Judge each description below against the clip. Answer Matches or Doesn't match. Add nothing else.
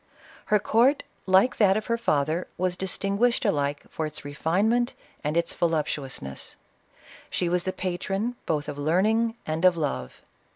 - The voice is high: Doesn't match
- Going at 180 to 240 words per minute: Doesn't match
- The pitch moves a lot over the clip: Matches